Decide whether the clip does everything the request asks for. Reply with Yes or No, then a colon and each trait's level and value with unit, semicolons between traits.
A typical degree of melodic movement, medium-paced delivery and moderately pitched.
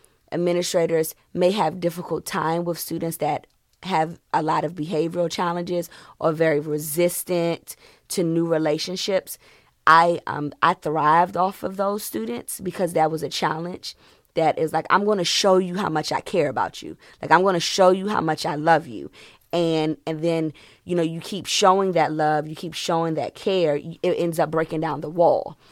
No: narrow, 2.2 semitones; average, 180 wpm; medium, 165 Hz